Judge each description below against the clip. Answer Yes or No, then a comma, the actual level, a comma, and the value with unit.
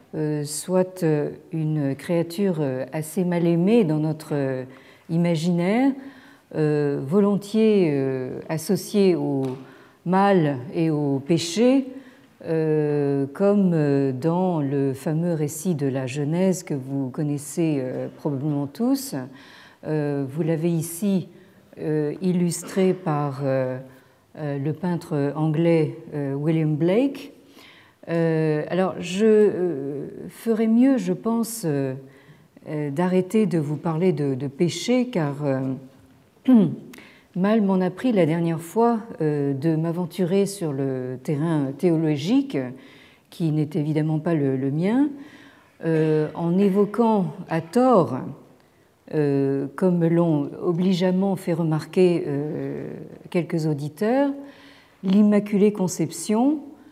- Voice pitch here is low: No, medium, 165 Hz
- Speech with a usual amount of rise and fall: Yes, average, 4.5 semitones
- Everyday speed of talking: No, slow, 95 wpm